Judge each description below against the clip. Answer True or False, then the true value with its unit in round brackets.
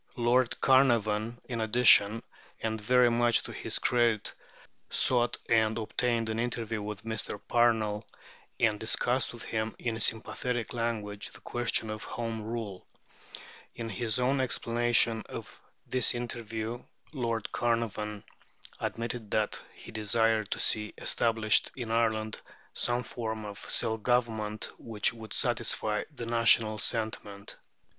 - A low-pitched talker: True (115 Hz)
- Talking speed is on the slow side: True (125 wpm)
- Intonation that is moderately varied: False (1.7 semitones)